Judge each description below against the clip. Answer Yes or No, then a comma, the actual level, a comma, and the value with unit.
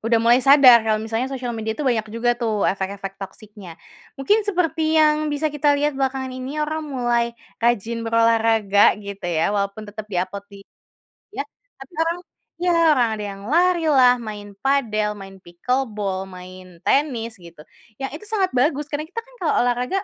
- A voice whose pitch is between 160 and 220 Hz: No, high, 235 Hz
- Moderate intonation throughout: No, wide, 5.8 semitones